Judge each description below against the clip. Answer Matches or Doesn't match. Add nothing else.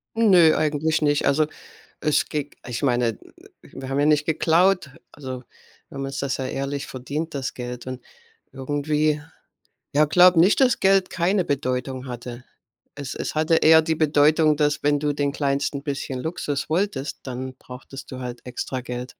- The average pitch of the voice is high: Doesn't match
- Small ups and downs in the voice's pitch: Doesn't match